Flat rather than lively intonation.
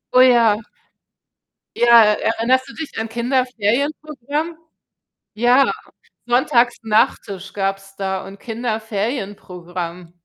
No: average, 4.2 semitones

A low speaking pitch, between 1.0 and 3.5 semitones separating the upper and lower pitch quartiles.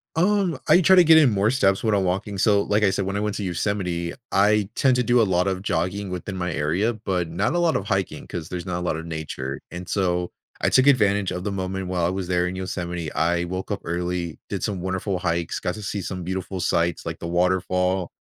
Yes: very low, 95 Hz; average, 2.7 semitones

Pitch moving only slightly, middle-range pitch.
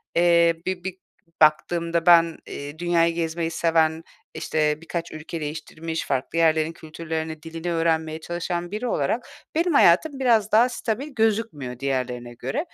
Yes: narrow, 2.0 semitones; medium, 165 Hz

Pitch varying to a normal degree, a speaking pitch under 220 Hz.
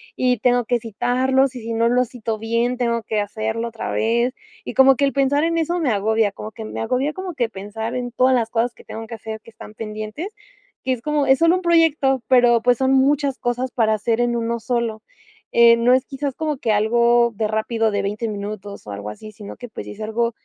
No: average, 3.0 semitones; high, 235 Hz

